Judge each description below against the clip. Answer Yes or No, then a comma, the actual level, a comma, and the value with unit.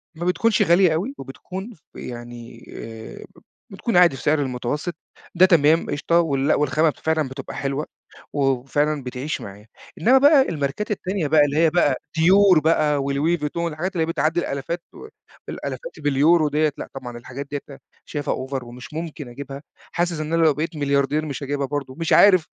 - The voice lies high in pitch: No, medium, 150 Hz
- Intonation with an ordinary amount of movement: Yes, average, 3.7 semitones